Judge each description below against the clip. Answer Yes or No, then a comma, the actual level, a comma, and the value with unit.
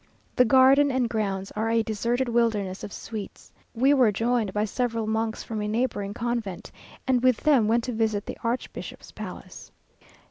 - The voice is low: No, high, 230 Hz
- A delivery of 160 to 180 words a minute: Yes, average, 170 wpm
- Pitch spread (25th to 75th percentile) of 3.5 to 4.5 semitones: No, average, 2.7 semitones